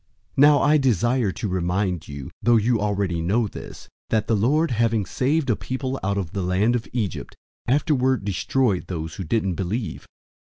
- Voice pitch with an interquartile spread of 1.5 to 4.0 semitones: No, average, 5.2 semitones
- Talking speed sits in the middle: Yes, average, 175 wpm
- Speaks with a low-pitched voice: Yes, low, 110 Hz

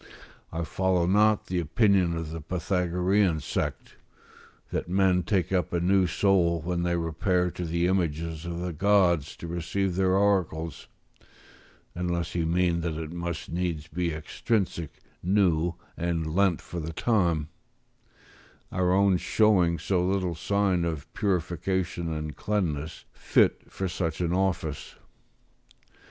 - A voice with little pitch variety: Yes, narrow, 2.2 semitones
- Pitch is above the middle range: No, very low, 85 Hz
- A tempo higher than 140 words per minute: No, slow, 135 wpm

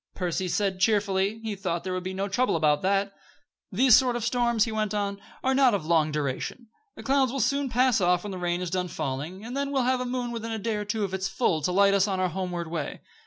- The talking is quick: Yes, fast, 260 wpm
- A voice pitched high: Yes, high, 200 Hz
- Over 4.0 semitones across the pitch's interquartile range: Yes, average, 4.7 semitones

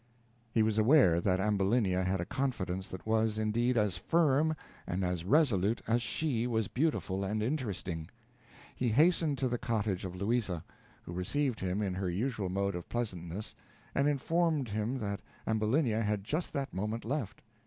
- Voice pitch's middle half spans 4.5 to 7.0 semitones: Yes, average, 5.2 semitones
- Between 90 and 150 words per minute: No, average, 165 wpm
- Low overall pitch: Yes, low, 110 Hz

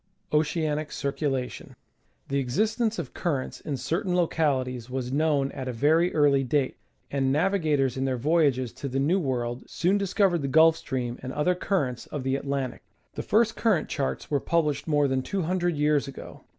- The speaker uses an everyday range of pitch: Yes, average, 4.0 semitones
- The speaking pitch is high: No, medium, 145 Hz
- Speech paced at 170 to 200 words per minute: Yes, average, 180 wpm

